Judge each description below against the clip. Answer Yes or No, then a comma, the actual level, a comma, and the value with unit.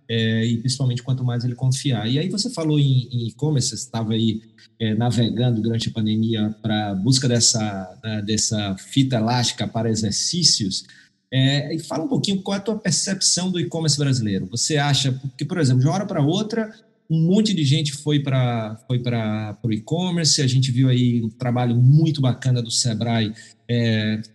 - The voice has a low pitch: Yes, low, 125 Hz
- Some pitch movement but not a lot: Yes, average, 4.9 semitones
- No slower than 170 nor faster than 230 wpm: Yes, average, 180 wpm